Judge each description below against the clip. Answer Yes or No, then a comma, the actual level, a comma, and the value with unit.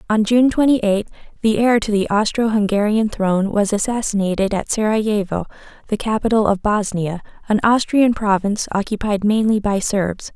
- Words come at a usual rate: Yes, average, 150 wpm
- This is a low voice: No, high, 210 Hz